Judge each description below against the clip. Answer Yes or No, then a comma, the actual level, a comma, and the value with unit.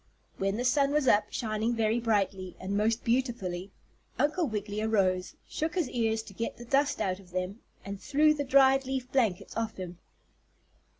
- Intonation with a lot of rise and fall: No, average, 5.0 semitones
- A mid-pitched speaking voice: No, high, 225 Hz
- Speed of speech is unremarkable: Yes, average, 175 wpm